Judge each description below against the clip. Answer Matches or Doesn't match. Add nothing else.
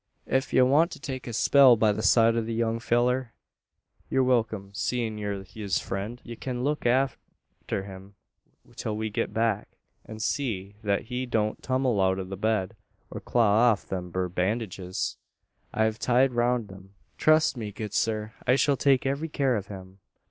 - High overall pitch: Doesn't match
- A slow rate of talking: Doesn't match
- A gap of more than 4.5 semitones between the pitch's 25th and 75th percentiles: Doesn't match